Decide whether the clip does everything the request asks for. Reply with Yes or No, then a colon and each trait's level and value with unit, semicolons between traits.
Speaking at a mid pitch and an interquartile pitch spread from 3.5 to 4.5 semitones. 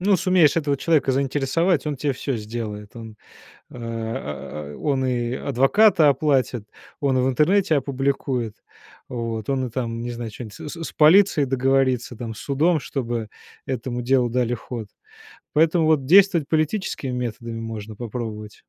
No: low, 130 Hz; average, 4.2 semitones